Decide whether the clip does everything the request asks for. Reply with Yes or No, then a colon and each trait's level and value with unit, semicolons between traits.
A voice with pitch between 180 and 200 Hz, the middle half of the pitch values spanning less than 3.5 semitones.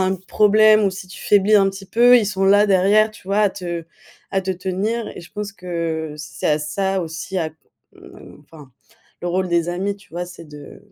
Yes: high, 190 Hz; average, 2.9 semitones